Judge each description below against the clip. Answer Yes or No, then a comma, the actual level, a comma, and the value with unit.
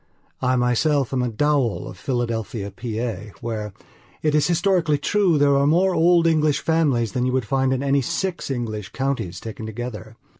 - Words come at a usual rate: Yes, average, 175 wpm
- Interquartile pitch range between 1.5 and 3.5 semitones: No, average, 4.9 semitones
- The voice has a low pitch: Yes, low, 130 Hz